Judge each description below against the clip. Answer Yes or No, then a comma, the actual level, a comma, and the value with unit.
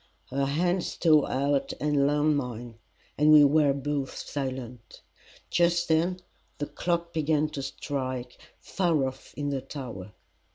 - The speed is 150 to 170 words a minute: No, average, 140 wpm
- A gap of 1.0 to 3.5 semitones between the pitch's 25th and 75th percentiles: Yes, average, 2.8 semitones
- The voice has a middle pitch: Yes, medium, 145 Hz